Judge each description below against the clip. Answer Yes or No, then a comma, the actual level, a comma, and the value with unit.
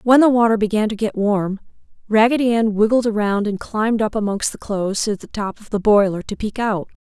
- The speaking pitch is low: No, high, 215 Hz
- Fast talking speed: Yes, fast, 220 wpm